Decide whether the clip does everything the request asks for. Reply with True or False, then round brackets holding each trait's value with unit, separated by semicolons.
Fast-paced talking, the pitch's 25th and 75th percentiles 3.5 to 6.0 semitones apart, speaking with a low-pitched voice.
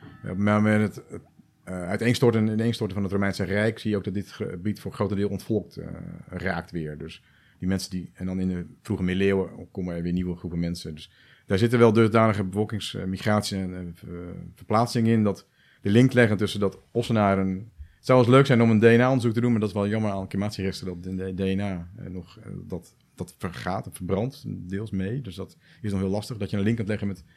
False (210 wpm; 3.1 semitones; 100 Hz)